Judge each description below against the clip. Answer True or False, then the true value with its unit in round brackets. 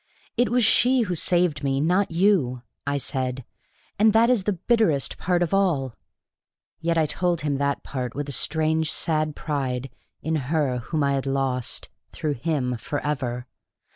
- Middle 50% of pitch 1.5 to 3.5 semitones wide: False (4.7 semitones)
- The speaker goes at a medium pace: True (165 wpm)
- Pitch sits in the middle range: True (150 Hz)